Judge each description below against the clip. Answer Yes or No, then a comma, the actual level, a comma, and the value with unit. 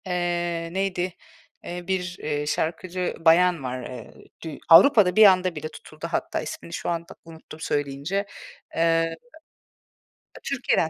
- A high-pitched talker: No, medium, 170 Hz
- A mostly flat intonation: Yes, narrow, 2.3 semitones